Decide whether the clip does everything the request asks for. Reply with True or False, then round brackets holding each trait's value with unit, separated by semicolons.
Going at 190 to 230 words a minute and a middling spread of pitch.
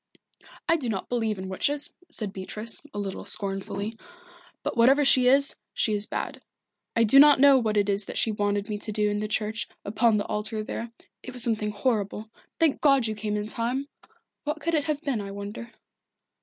True (200 wpm; 4.0 semitones)